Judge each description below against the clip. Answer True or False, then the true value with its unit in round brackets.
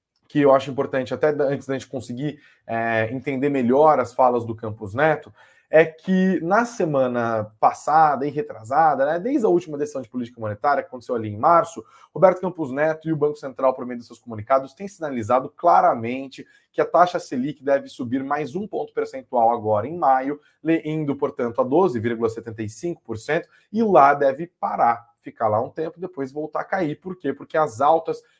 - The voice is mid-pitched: True (145 Hz)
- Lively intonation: False (4.6 semitones)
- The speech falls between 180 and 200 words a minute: True (185 wpm)